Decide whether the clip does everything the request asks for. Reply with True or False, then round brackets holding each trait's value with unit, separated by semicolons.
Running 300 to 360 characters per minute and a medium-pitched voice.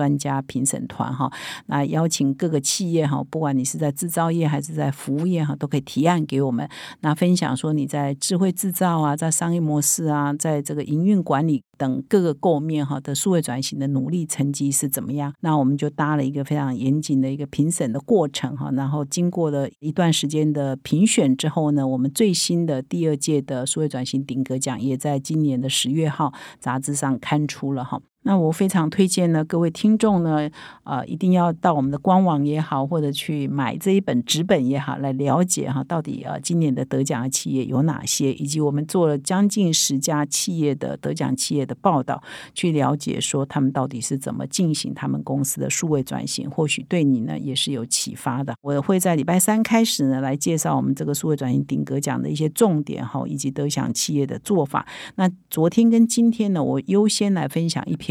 True (315 characters per minute; 150 Hz)